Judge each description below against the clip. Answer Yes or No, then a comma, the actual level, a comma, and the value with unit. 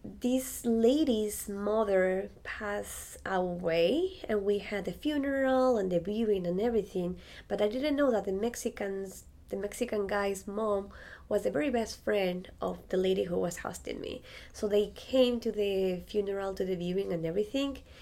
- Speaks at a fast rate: No, average, 165 wpm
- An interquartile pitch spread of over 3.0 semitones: Yes, average, 3.7 semitones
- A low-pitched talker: No, high, 205 Hz